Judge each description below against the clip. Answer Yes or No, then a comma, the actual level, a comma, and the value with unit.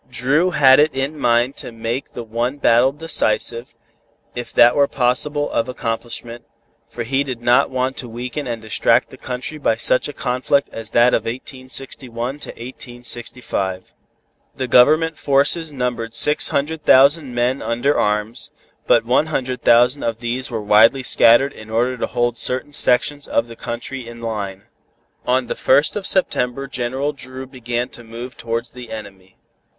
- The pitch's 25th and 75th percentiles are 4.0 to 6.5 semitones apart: No, average, 2.7 semitones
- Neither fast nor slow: Yes, average, 165 wpm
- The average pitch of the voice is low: Yes, low, 125 Hz